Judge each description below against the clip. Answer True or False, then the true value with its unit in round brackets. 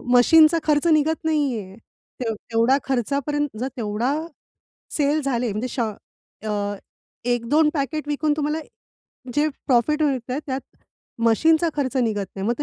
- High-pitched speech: True (275 Hz)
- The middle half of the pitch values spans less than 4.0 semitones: False (4.3 semitones)